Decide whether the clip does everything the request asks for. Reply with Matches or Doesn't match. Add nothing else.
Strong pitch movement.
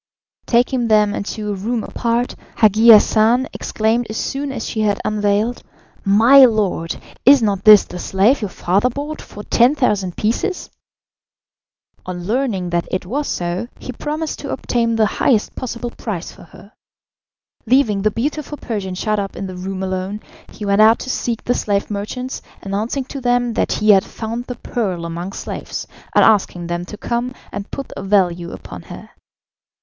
Doesn't match